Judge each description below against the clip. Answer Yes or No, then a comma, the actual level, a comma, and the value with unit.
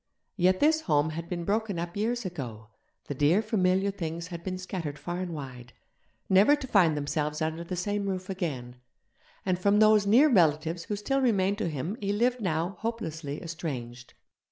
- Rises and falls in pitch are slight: No, average, 4.5 semitones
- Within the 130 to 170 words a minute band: No, average, 180 wpm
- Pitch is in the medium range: Yes, medium, 180 Hz